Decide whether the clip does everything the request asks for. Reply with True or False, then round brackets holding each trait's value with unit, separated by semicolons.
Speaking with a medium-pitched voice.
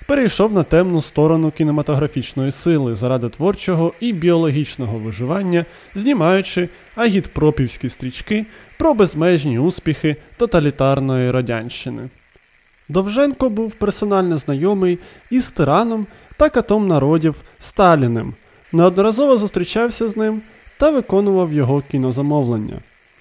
True (170 Hz)